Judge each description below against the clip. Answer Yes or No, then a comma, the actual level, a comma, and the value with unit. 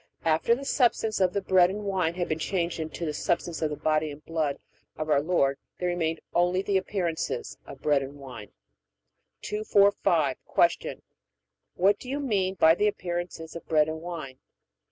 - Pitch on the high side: No, medium, 170 Hz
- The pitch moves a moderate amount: Yes, average, 3.6 semitones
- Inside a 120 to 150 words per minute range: No, average, 175 wpm